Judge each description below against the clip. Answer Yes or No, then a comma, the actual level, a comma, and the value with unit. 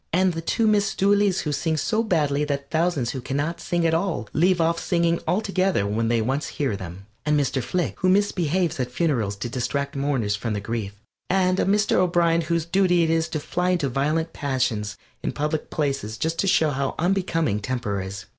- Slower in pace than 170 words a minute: No, average, 200 wpm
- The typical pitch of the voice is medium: Yes, medium, 155 Hz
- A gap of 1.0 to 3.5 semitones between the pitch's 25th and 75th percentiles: No, wide, 5.5 semitones